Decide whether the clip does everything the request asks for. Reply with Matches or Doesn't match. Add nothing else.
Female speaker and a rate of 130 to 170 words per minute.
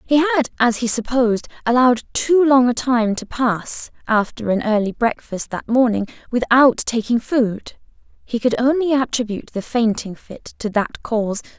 Matches